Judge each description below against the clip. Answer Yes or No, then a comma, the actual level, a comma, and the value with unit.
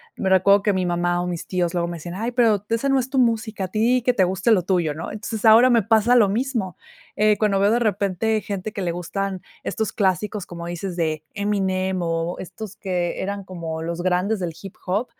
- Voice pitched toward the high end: Yes, high, 195 Hz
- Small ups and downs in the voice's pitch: No, average, 3.6 semitones